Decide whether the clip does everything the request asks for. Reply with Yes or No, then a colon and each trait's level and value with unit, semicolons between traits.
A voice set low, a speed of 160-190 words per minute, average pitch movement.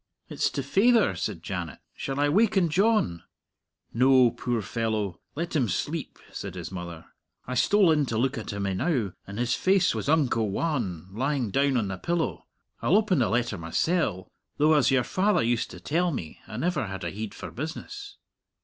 No: low, 130 Hz; average, 185 wpm; wide, 8.2 semitones